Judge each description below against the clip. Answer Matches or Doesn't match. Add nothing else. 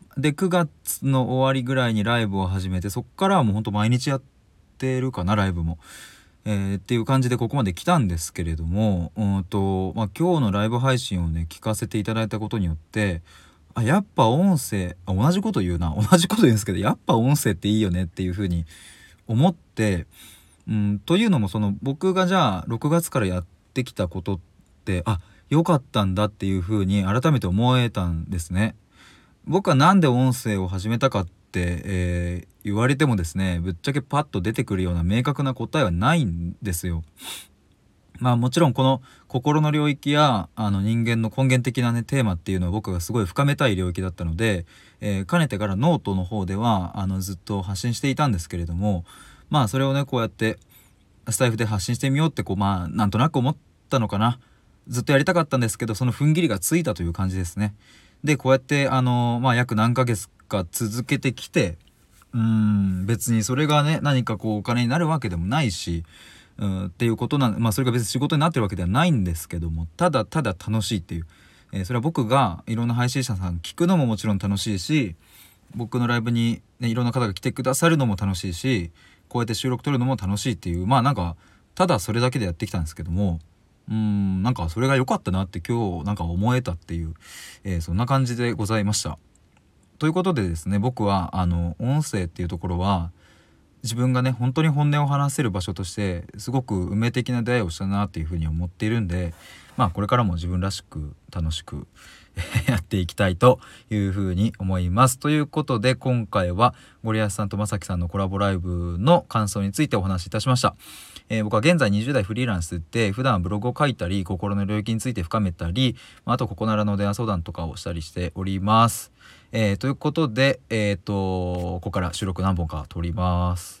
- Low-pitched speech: Matches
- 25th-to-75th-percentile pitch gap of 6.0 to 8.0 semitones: Doesn't match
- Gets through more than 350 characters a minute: Matches